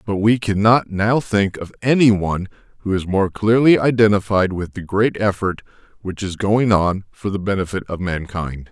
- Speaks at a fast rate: No, average, 180 wpm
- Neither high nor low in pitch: No, low, 100 Hz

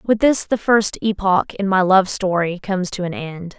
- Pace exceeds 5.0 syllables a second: No, 4.6 syllables/s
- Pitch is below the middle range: No, high, 190 Hz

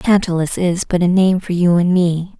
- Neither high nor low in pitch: Yes, medium, 180 Hz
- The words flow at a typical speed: No, fast, 225 wpm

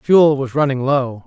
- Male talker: Yes, male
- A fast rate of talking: No, average, 190 wpm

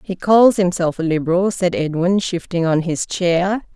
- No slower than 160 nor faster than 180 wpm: Yes, average, 175 wpm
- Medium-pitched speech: Yes, medium, 180 Hz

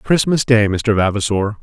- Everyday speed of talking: Yes, average, 150 wpm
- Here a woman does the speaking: No, male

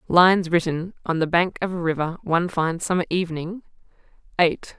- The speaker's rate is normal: Yes, average, 165 wpm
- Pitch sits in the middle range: Yes, medium, 170 Hz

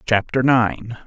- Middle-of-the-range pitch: No, low, 115 Hz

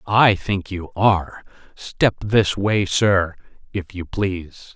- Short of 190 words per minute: Yes, average, 140 wpm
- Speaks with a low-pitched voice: Yes, very low, 95 Hz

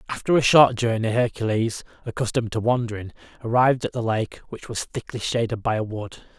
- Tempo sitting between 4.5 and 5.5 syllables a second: No, 5.8 syllables/s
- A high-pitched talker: No, low, 115 Hz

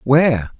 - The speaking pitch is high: No, low, 135 Hz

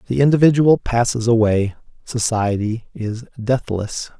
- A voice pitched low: Yes, low, 115 Hz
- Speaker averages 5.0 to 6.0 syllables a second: No, 4.3 syllables/s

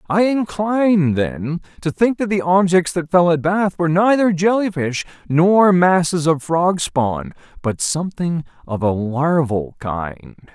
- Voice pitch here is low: No, medium, 165 Hz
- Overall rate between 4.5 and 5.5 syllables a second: No, 4.0 syllables/s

